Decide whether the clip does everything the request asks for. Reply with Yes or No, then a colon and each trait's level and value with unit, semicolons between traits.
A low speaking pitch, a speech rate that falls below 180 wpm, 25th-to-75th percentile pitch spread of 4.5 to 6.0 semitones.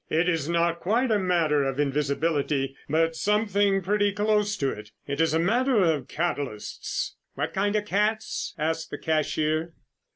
No: medium, 165 Hz; average, 160 wpm; wide, 5.4 semitones